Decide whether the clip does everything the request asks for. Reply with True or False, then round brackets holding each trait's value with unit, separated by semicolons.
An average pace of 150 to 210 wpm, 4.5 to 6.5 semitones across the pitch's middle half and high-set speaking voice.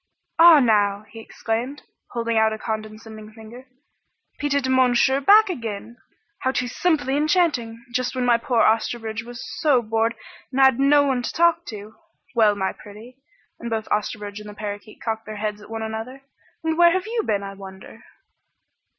False (170 wpm; 3.8 semitones; 230 Hz)